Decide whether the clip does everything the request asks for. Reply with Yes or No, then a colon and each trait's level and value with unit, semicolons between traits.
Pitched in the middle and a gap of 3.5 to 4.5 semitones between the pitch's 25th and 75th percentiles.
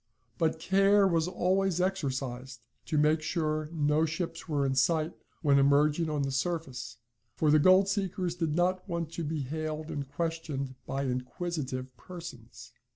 Yes: medium, 155 Hz; average, 3.8 semitones